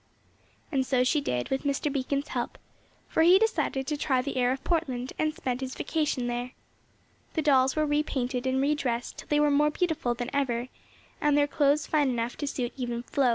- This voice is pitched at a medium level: No, very high, 270 Hz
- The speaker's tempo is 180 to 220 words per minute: Yes, fast, 205 wpm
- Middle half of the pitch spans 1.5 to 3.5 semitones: Yes, average, 2.9 semitones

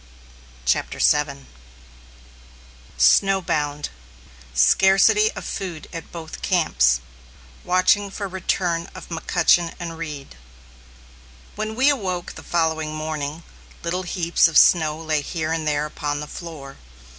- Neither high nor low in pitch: Yes, medium, 165 Hz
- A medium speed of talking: No, slow, 120 wpm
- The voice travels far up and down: No, average, 3.5 semitones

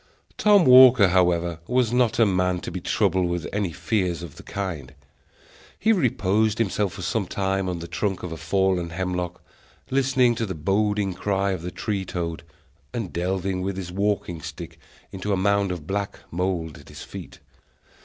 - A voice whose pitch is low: Yes, very low, 95 Hz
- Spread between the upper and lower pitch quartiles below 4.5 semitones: Yes, average, 2.9 semitones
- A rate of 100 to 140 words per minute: No, average, 175 wpm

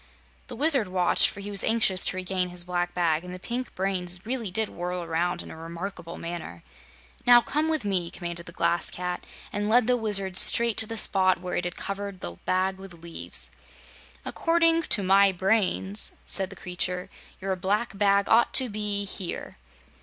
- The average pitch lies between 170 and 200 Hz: Yes, high, 190 Hz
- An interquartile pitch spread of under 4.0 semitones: Yes, average, 3.1 semitones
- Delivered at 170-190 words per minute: Yes, average, 185 wpm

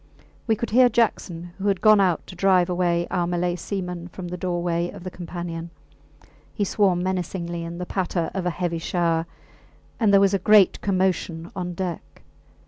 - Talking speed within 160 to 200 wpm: Yes, average, 180 wpm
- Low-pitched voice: No, medium, 180 Hz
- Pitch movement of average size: No, narrow, 2.0 semitones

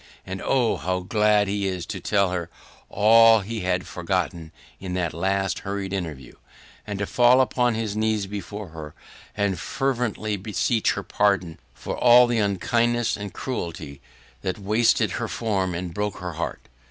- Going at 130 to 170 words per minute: Yes, average, 160 wpm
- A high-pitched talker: No, low, 100 Hz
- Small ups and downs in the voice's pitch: No, average, 3.2 semitones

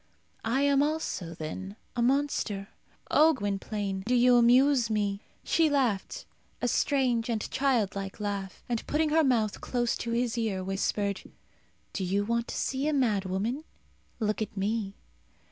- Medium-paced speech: Yes, average, 150 wpm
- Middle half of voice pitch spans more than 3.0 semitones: Yes, average, 4.7 semitones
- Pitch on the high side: Yes, high, 230 Hz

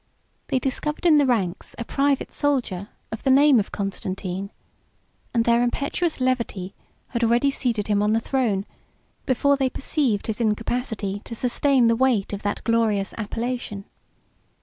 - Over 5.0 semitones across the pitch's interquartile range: No, average, 4.2 semitones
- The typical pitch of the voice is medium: No, high, 235 Hz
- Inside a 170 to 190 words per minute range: No, average, 150 wpm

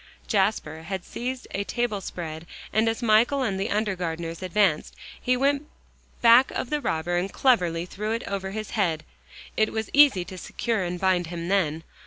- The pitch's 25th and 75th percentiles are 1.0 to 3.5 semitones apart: No, average, 4.8 semitones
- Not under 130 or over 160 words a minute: No, average, 175 wpm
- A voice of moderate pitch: No, high, 195 Hz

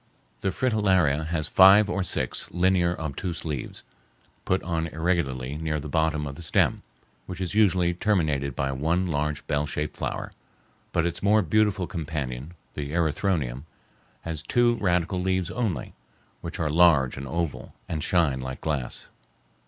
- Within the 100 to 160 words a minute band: Yes, average, 150 wpm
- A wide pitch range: No, average, 3.9 semitones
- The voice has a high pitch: No, very low, 80 Hz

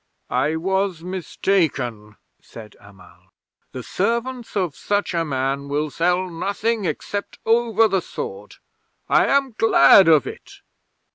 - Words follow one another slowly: Yes, slow, 125 wpm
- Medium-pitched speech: Yes, medium, 180 Hz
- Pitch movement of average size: No, wide, 6.8 semitones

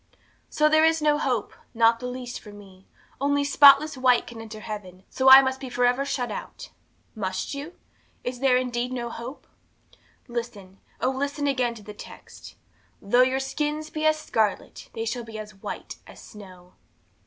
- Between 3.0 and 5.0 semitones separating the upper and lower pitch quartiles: Yes, average, 4.1 semitones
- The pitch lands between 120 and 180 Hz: No, very high, 250 Hz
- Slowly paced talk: No, average, 175 wpm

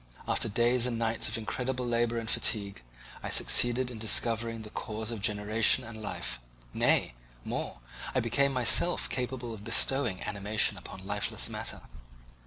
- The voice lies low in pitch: Yes, low, 115 Hz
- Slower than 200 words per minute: Yes, average, 150 wpm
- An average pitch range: No, narrow, 2.1 semitones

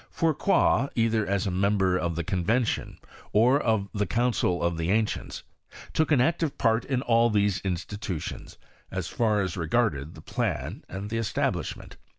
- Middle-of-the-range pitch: No, low, 105 Hz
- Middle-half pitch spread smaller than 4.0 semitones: No, average, 4.3 semitones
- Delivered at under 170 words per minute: Yes, average, 160 wpm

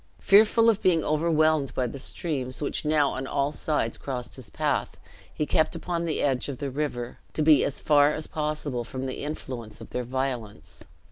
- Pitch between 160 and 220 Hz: No, medium, 145 Hz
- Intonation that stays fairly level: No, average, 3.2 semitones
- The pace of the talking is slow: No, average, 190 wpm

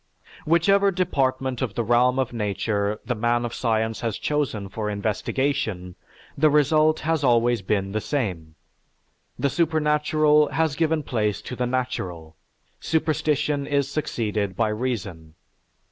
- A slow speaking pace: Yes, slow, 130 wpm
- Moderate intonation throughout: No, wide, 5.9 semitones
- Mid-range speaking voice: No, low, 125 Hz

